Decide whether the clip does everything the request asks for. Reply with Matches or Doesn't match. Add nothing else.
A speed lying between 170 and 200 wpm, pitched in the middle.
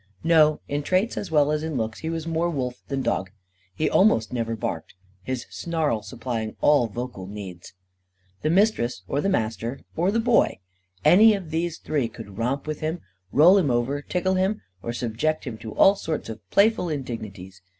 Matches